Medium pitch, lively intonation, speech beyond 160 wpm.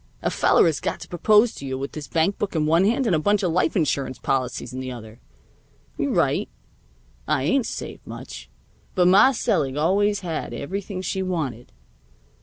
Yes: medium, 170 Hz; wide, 6.3 semitones; average, 190 wpm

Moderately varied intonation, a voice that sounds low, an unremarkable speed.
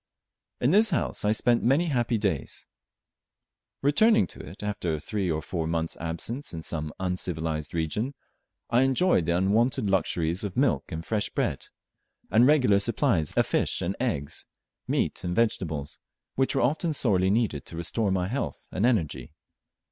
No: wide, 6.8 semitones; low, 100 Hz; average, 160 wpm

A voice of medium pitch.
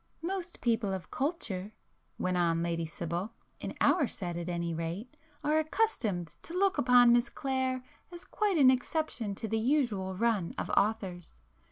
No: high, 225 Hz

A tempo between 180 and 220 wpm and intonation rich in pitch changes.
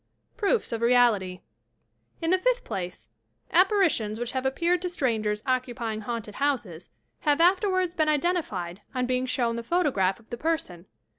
No: average, 150 wpm; wide, 7.7 semitones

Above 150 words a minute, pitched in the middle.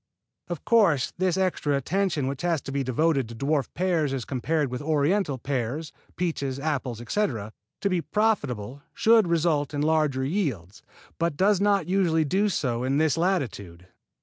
Yes: average, 160 wpm; medium, 150 Hz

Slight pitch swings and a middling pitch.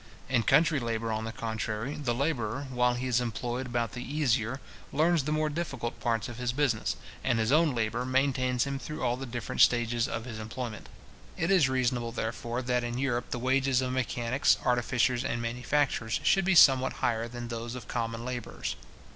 No: narrow, 2.3 semitones; low, 125 Hz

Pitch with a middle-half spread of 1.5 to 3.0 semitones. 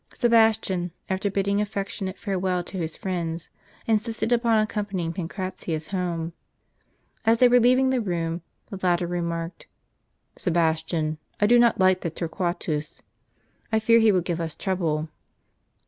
No: average, 4.3 semitones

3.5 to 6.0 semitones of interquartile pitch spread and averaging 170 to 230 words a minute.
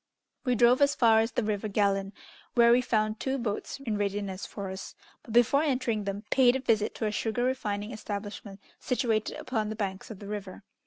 No: average, 3.0 semitones; average, 200 wpm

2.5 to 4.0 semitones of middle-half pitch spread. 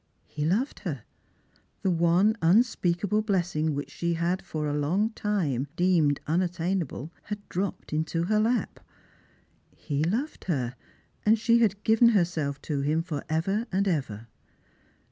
No: average, 5.1 semitones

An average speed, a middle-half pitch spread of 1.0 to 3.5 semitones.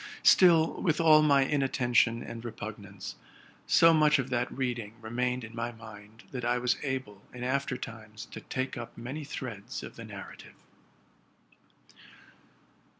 Yes: average, 150 wpm; average, 3.1 semitones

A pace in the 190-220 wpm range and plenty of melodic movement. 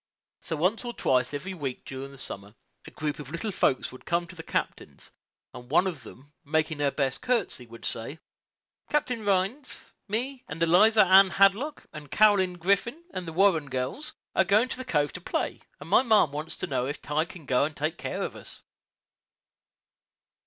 Yes: average, 195 wpm; wide, 6.1 semitones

